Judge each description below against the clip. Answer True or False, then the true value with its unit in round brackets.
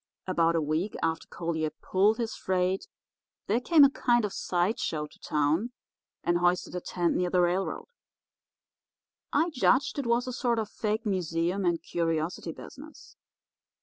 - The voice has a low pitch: False (185 Hz)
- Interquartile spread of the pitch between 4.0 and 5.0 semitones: False (5.6 semitones)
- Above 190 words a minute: False (155 wpm)